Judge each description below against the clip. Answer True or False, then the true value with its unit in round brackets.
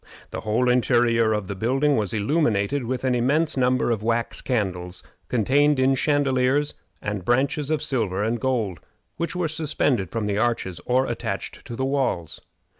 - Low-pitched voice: True (125 Hz)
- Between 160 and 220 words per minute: True (165 wpm)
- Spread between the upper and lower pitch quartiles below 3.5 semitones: False (4.3 semitones)